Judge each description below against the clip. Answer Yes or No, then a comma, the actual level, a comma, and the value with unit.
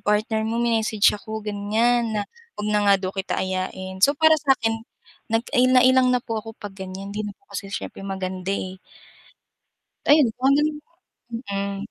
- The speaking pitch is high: Yes, high, 215 Hz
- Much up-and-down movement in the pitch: No, average, 3.4 semitones